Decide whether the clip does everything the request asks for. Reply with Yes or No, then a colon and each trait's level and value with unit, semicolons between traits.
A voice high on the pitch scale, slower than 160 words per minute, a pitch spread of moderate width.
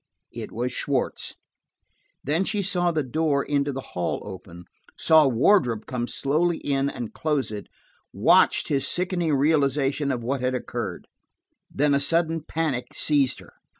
No: medium, 140 Hz; average, 150 wpm; average, 4.0 semitones